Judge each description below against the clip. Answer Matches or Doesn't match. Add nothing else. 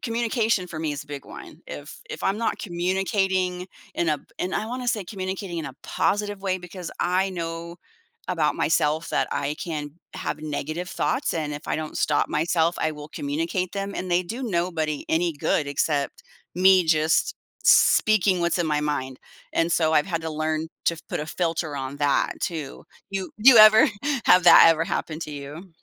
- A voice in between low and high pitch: Matches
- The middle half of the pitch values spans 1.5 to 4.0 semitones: Matches